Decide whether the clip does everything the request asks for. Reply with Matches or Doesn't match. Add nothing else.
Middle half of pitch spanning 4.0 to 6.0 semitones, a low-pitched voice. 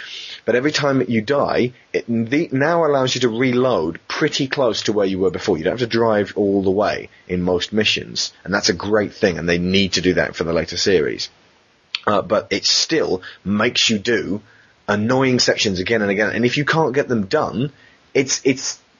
Matches